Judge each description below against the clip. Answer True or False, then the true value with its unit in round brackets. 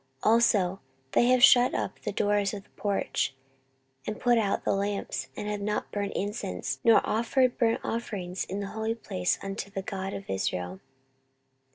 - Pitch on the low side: False (205 Hz)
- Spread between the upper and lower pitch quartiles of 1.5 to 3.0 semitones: True (2.7 semitones)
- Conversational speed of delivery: True (175 wpm)